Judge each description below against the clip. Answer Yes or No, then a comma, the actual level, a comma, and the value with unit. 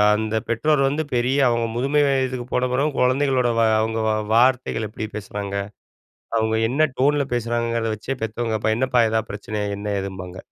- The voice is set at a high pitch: No, low, 120 Hz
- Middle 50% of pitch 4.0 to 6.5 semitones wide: No, average, 3.2 semitones